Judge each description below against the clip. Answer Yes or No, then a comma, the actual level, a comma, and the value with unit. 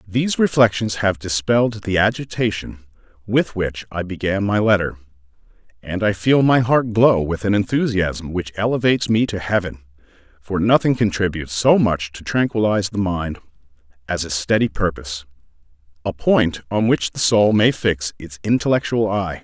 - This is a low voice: Yes, low, 100 Hz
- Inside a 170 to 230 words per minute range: No, average, 150 wpm